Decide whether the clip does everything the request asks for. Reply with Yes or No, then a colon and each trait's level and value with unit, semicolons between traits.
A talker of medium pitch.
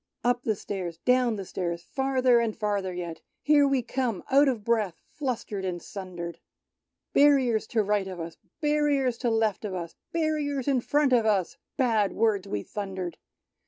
No: high, 225 Hz